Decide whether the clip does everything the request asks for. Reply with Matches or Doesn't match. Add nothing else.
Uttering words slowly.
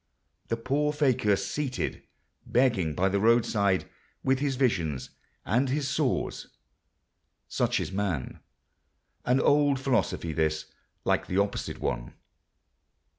Matches